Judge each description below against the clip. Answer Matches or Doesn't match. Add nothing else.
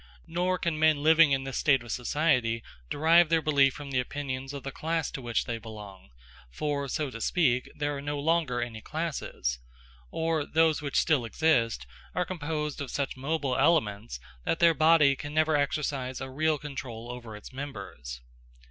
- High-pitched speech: Doesn't match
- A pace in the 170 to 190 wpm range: Matches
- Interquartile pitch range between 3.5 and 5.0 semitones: Matches